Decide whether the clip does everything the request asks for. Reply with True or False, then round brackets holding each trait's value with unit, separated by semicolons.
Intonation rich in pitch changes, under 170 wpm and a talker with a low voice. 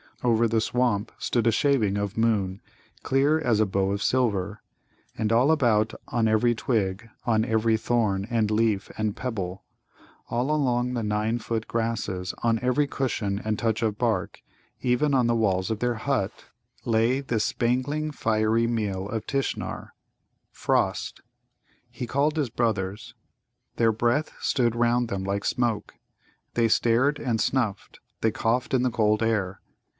False (2.4 semitones; 150 wpm; 115 Hz)